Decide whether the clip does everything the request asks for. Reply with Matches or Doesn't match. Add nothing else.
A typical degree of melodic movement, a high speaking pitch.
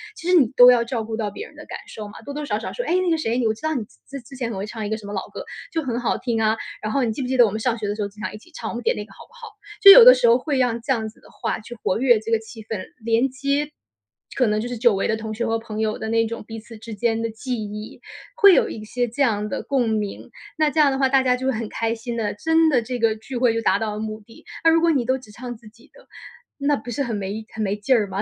Matches